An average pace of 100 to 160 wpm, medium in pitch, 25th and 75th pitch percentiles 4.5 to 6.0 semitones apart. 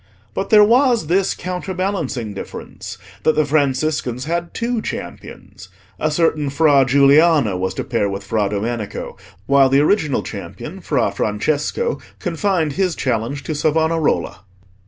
Yes: slow, 135 wpm; medium, 150 Hz; average, 5.3 semitones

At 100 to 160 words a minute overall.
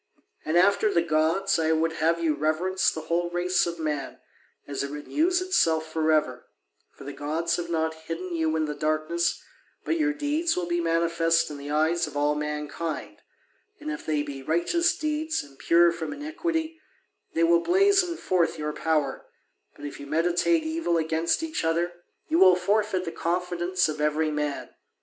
No: average, 175 wpm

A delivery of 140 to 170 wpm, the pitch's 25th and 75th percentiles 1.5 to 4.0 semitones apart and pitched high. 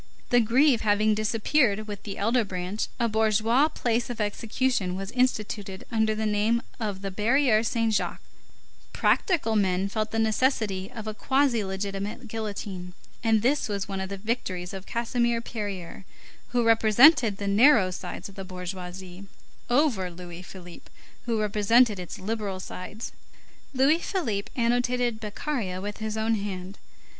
Yes: average, 150 wpm; average, 3.3 semitones; high, 215 Hz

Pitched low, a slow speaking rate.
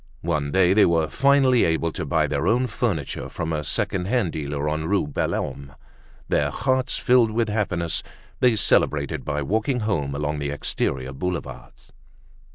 No: very low, 85 Hz; average, 160 wpm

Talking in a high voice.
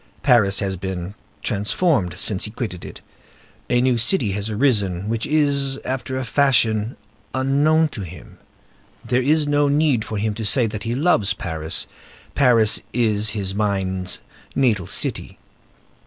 No: low, 110 Hz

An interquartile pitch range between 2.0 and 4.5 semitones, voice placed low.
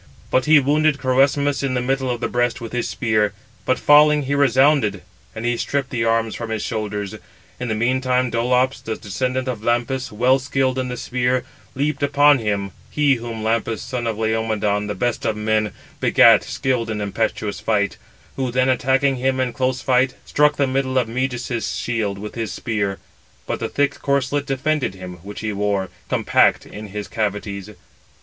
Yes: average, 3.4 semitones; low, 125 Hz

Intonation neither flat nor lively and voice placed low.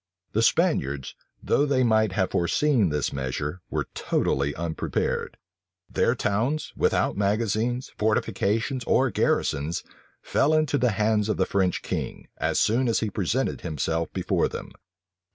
No: wide, 6.0 semitones; low, 105 Hz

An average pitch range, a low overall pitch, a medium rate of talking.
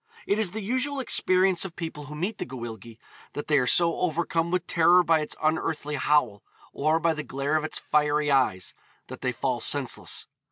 No: average, 3.3 semitones; medium, 155 Hz; average, 195 wpm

